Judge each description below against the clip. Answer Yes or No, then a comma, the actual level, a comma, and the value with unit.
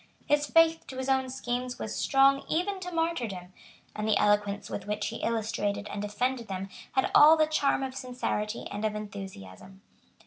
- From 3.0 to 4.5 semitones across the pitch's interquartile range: No, average, 4.9 semitones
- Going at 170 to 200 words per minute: Yes, average, 175 wpm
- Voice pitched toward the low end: No, high, 240 Hz